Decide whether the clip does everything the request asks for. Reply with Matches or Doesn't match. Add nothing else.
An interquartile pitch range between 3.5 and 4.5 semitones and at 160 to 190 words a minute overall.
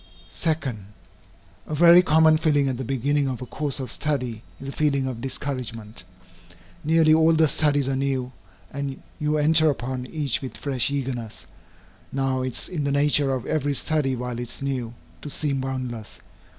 Doesn't match